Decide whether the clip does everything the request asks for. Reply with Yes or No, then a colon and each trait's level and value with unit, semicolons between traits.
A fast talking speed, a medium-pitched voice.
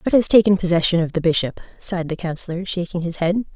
Yes: fast, 220 wpm; medium, 180 Hz